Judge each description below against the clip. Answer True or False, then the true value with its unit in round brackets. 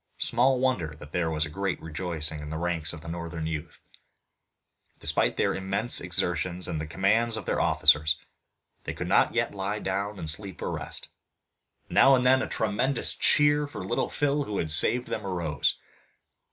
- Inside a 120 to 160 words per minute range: False (170 wpm)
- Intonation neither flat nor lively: False (5.8 semitones)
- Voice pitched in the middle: False (90 Hz)